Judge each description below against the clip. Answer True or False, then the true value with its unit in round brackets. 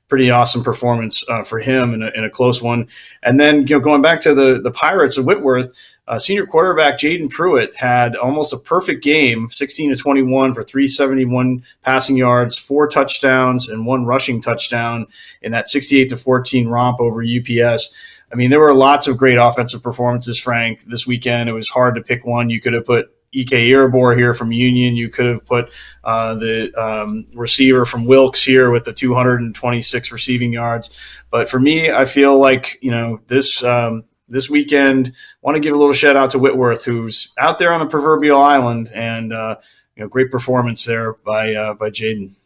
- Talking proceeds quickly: False (195 wpm)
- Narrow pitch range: True (2.3 semitones)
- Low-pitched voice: True (125 Hz)